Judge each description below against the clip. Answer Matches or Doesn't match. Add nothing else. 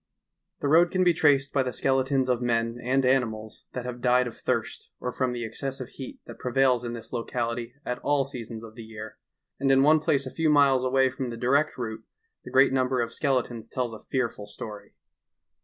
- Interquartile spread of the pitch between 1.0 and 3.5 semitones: Matches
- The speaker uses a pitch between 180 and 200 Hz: Doesn't match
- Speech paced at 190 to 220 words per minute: Matches